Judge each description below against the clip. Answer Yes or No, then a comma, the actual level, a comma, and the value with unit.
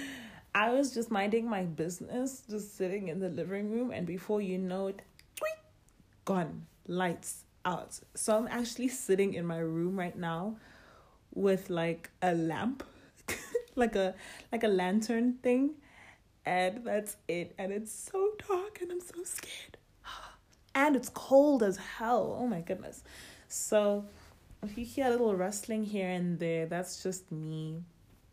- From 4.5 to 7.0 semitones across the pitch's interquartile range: Yes, average, 4.9 semitones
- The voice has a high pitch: Yes, high, 205 Hz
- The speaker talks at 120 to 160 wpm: Yes, average, 150 wpm